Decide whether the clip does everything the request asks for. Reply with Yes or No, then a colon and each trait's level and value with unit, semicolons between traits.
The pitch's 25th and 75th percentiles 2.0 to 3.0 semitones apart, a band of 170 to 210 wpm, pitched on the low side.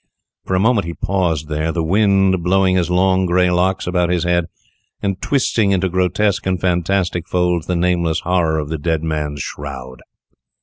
Yes: narrow, 2.4 semitones; average, 175 wpm; very low, 90 Hz